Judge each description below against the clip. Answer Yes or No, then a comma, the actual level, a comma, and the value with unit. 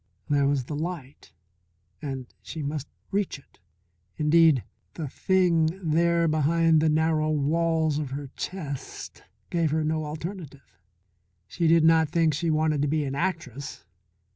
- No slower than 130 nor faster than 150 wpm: Yes, average, 140 wpm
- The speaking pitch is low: No, medium, 155 Hz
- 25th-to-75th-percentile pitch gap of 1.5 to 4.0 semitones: Yes, narrow, 2.4 semitones